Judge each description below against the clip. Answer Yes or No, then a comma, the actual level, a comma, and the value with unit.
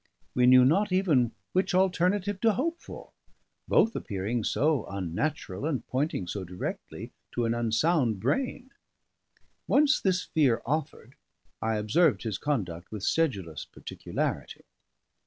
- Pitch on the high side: No, low, 135 Hz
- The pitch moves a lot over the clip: Yes, wide, 8.8 semitones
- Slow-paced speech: Yes, slow, 125 wpm